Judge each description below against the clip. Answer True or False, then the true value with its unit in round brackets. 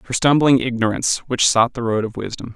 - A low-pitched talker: True (120 Hz)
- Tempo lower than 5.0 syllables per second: False (6.1 syllables/s)